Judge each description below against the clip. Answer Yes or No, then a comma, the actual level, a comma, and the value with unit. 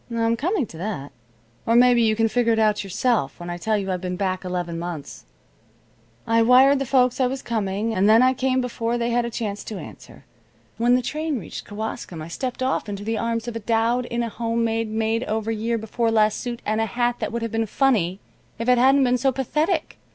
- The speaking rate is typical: No, fast, 230 wpm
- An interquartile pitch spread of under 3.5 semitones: Yes, average, 2.7 semitones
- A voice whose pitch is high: Yes, high, 230 Hz